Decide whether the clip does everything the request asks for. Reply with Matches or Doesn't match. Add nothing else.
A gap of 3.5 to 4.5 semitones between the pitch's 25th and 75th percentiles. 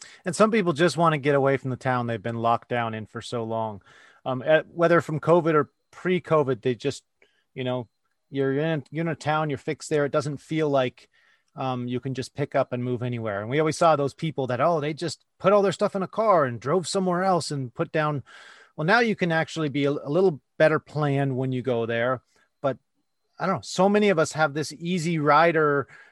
Matches